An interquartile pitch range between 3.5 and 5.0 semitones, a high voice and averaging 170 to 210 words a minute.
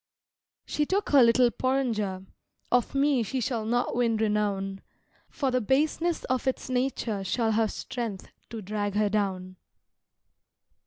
No: average, 3.8 semitones; high, 230 Hz; average, 140 wpm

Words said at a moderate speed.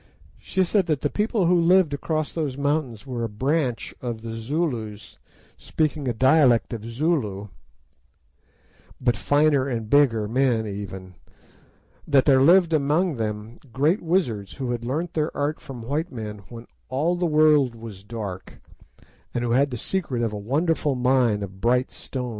Yes: average, 160 wpm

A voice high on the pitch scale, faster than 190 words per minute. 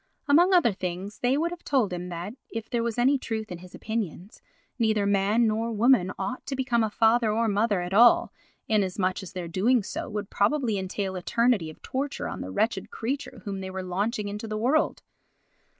Yes: high, 215 Hz; average, 200 wpm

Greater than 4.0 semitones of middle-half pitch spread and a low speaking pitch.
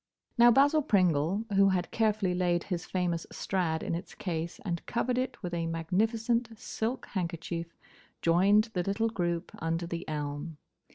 No: average, 4.5 semitones; medium, 180 Hz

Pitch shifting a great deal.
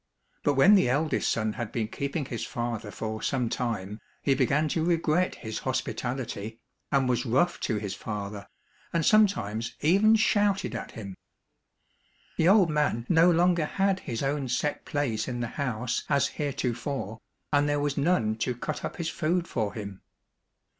Yes: wide, 6.0 semitones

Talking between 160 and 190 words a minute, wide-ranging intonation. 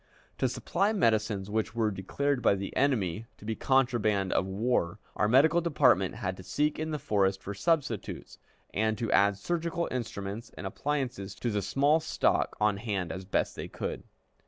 Yes: average, 175 wpm; wide, 5.8 semitones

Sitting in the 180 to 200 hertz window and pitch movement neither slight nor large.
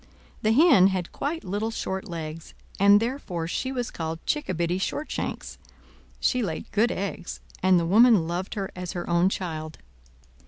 Yes: high, 190 Hz; average, 4.5 semitones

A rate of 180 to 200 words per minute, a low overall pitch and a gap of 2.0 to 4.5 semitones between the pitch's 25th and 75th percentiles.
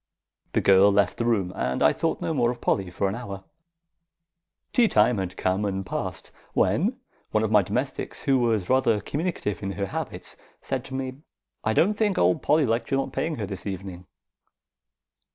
No: average, 190 wpm; low, 105 Hz; average, 5.3 semitones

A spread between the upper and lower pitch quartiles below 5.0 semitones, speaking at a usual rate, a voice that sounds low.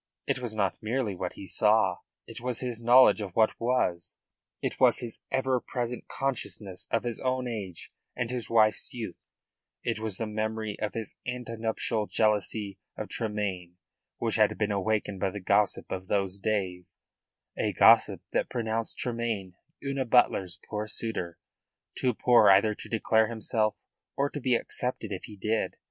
Yes: average, 2.9 semitones; average, 165 wpm; low, 110 Hz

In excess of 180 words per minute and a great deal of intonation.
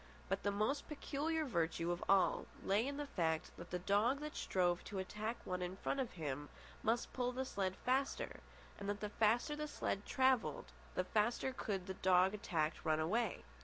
Yes: average, 190 wpm; wide, 5.7 semitones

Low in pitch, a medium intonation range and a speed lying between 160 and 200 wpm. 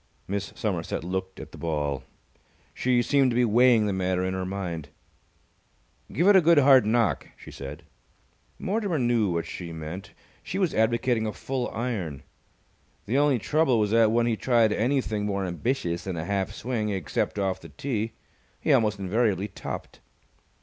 Yes: low, 110 Hz; average, 4.8 semitones; average, 170 wpm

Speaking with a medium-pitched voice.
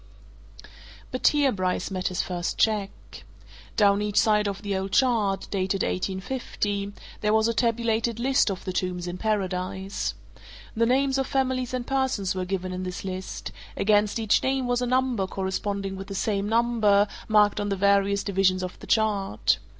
No: high, 205 Hz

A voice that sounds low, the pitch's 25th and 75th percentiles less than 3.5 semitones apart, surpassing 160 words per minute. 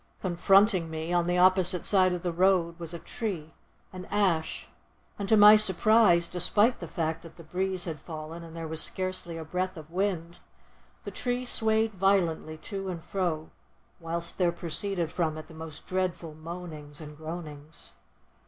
No: medium, 175 Hz; average, 2.7 semitones; average, 170 wpm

